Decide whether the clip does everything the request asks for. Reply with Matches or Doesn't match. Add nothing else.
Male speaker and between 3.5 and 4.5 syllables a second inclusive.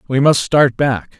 Matches